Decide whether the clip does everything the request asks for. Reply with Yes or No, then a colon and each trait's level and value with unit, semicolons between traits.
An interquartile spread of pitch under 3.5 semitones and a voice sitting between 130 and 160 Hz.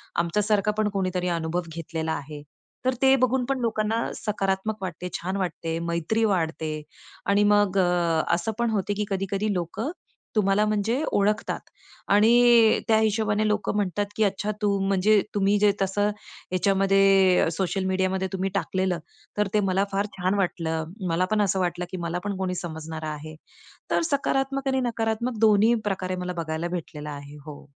No: average, 3.1 semitones; high, 195 Hz